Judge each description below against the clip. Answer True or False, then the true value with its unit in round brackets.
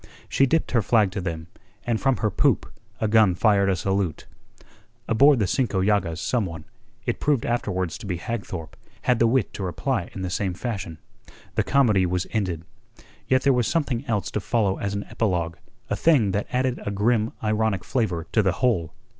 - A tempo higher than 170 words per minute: True (190 wpm)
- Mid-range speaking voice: False (105 Hz)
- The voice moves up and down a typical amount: True (4.4 semitones)